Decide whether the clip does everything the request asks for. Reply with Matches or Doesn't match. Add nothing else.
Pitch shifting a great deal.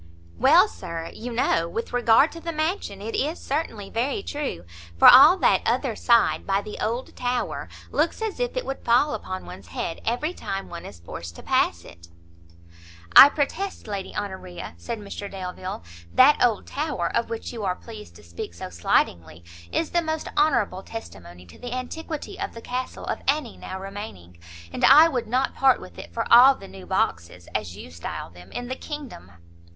Matches